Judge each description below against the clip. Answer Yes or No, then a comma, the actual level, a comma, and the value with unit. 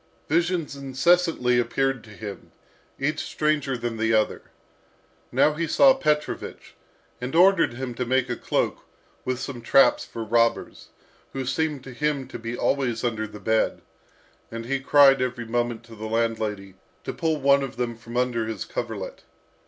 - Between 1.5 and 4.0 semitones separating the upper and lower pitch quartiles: Yes, average, 3.5 semitones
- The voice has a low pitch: Yes, low, 125 Hz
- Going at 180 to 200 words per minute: No, average, 160 wpm